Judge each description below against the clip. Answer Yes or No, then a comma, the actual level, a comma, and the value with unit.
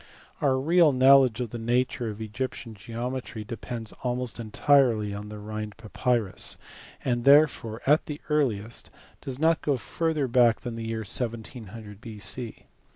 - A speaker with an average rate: Yes, average, 145 wpm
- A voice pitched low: Yes, low, 120 Hz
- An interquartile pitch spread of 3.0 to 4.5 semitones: Yes, average, 3.3 semitones